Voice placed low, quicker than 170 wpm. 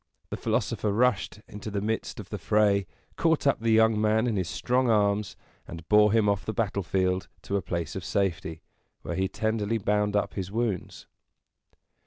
Yes: low, 105 Hz; average, 180 wpm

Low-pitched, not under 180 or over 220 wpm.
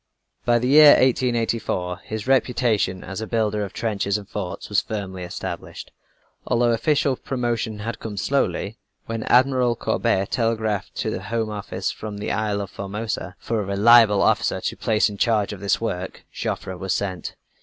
No: low, 110 Hz; average, 165 wpm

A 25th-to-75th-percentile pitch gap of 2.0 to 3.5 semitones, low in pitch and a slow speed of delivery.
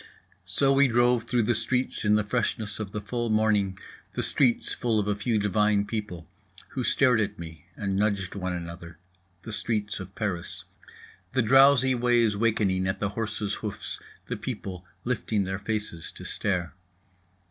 No: average, 3.1 semitones; low, 105 Hz; average, 165 wpm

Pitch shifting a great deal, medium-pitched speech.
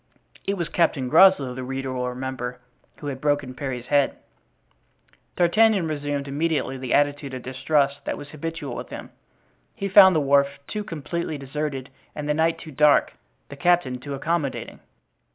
No: average, 3.4 semitones; medium, 145 Hz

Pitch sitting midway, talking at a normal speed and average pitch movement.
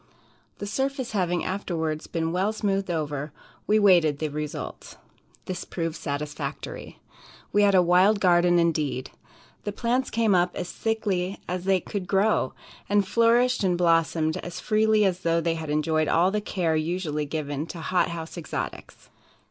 Yes: medium, 175 Hz; average, 155 wpm; average, 4.1 semitones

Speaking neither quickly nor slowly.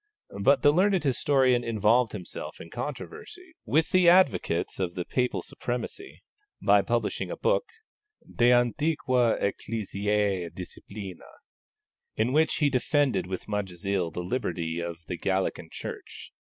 No: slow, 125 wpm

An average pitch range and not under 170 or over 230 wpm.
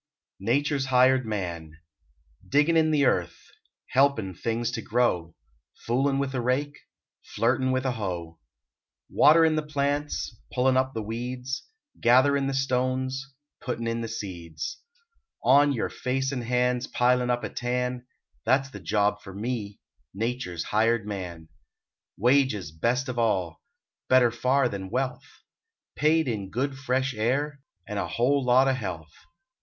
No: average, 3.9 semitones; average, 145 wpm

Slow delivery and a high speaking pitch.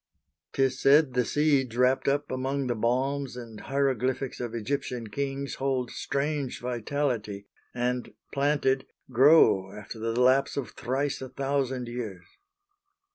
No: slow, 130 wpm; low, 130 Hz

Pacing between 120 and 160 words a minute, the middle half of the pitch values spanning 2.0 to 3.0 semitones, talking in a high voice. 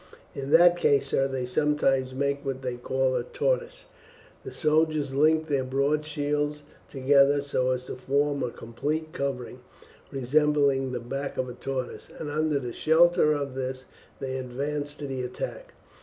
No: average, 155 wpm; narrow, 2.4 semitones; medium, 140 Hz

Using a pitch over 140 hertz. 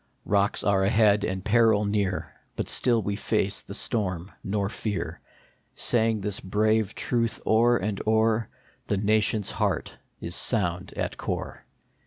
No: low, 105 Hz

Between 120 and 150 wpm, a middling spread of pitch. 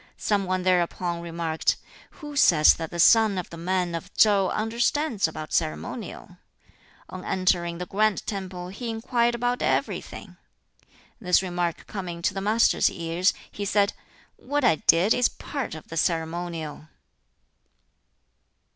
Yes: average, 140 wpm; average, 4.1 semitones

